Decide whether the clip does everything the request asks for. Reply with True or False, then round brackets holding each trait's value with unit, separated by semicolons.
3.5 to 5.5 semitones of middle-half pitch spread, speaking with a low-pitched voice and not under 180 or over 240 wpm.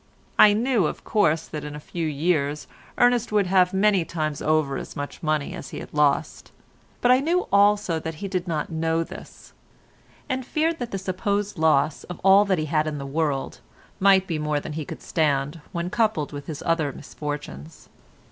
False (4.9 semitones; 165 Hz; 190 wpm)